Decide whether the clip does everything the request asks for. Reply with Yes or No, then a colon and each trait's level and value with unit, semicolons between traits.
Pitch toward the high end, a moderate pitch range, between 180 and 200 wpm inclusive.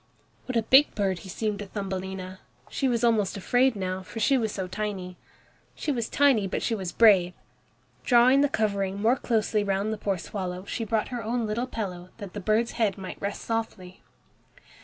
Yes: high, 210 Hz; average, 3.4 semitones; average, 190 wpm